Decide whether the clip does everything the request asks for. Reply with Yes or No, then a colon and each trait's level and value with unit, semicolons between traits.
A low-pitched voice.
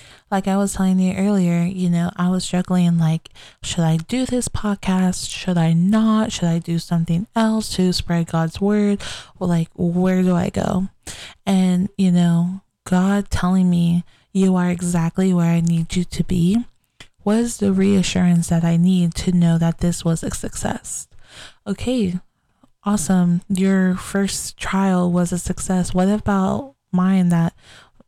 No: medium, 185 Hz